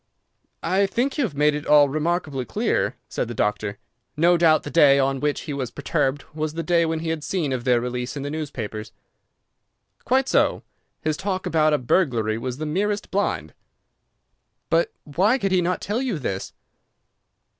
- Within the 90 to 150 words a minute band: No, average, 180 wpm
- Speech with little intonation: No, average, 5.1 semitones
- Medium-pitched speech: Yes, medium, 150 Hz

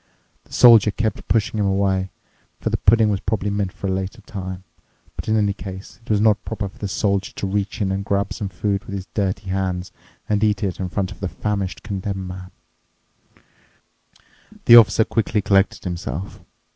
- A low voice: Yes, low, 100 Hz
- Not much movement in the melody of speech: Yes, narrow, 1.8 semitones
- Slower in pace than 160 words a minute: No, average, 190 wpm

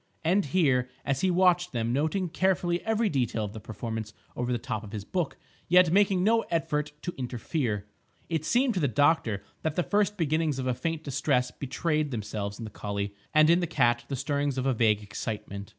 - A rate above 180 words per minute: Yes, average, 200 wpm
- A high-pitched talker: No, medium, 140 Hz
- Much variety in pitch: Yes, wide, 6.9 semitones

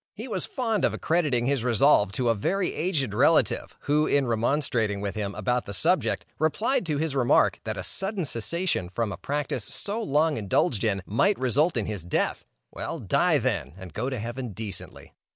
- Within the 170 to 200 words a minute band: Yes, average, 190 wpm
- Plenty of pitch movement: Yes, wide, 7.1 semitones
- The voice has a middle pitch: No, low, 130 Hz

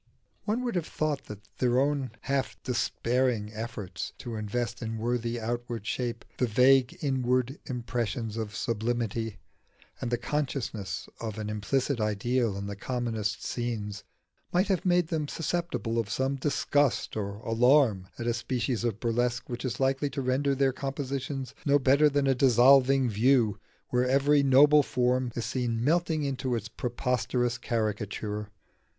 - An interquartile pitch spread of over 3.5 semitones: No, average, 3.2 semitones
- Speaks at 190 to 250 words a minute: No, average, 150 wpm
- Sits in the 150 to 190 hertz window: No, low, 125 Hz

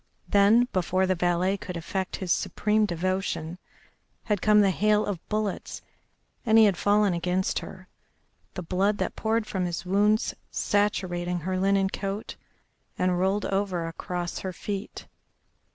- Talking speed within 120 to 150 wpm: Yes, average, 145 wpm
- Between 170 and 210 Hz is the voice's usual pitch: Yes, high, 190 Hz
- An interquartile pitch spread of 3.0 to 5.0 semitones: No, narrow, 2.4 semitones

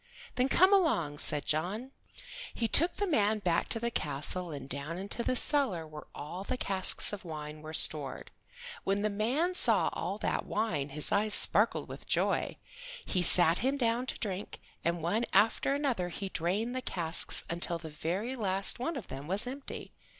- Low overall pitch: No, high, 195 Hz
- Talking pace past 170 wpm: Yes, average, 180 wpm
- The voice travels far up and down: Yes, wide, 6.5 semitones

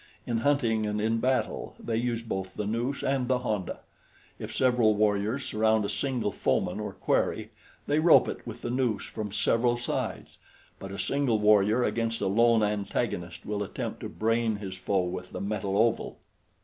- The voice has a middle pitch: No, low, 110 Hz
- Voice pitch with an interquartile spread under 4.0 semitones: Yes, average, 2.8 semitones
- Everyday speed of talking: Yes, average, 175 wpm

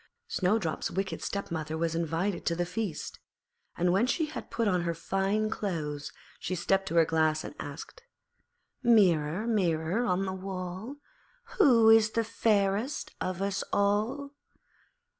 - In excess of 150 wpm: No, average, 140 wpm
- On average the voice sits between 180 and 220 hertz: Yes, high, 190 Hz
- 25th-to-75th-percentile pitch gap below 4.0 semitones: No, average, 4.5 semitones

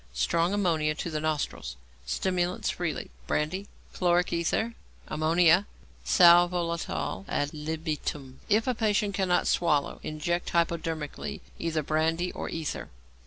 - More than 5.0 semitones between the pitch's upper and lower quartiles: No, narrow, 2.6 semitones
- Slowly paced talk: Yes, slow, 115 wpm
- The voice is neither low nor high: Yes, medium, 165 Hz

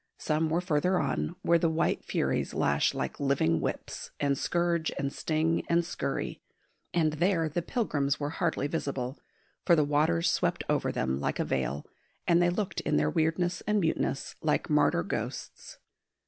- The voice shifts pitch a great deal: No, average, 3.6 semitones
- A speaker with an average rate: Yes, average, 165 wpm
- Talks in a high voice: No, medium, 160 Hz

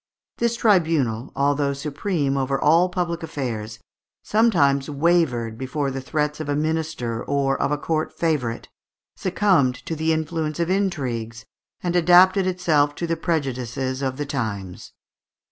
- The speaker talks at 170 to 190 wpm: No, average, 140 wpm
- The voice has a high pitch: No, medium, 150 Hz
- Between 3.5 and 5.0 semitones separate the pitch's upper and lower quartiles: Yes, average, 4.3 semitones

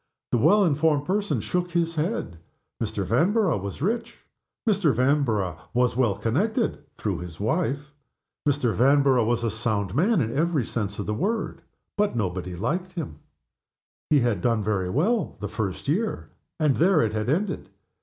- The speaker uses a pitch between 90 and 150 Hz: Yes, low, 135 Hz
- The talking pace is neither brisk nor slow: Yes, average, 165 wpm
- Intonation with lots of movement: Yes, wide, 8.4 semitones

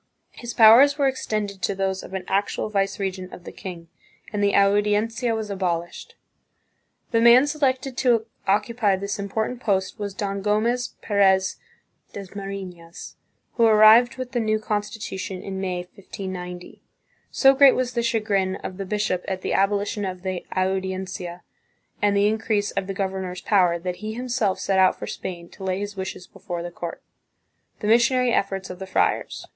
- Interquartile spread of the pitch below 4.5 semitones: Yes, average, 2.8 semitones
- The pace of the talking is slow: No, average, 165 wpm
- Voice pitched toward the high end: Yes, high, 200 Hz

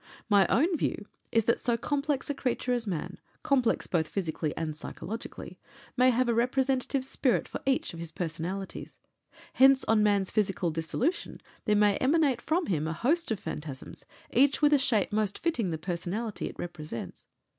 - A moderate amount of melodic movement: No, wide, 7.1 semitones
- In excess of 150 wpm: Yes, average, 170 wpm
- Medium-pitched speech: No, high, 225 Hz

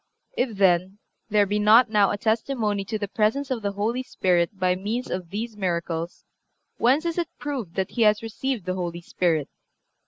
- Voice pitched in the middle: No, high, 210 Hz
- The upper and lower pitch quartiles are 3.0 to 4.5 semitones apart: Yes, average, 4.0 semitones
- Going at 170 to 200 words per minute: Yes, average, 185 wpm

